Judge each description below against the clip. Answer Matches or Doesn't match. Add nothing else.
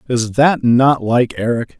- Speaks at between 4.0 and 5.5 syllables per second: Doesn't match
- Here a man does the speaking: Matches